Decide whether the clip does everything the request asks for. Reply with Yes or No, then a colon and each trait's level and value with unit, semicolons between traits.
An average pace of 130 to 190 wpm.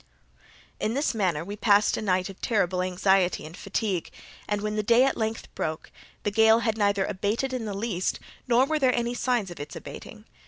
No: average, 200 wpm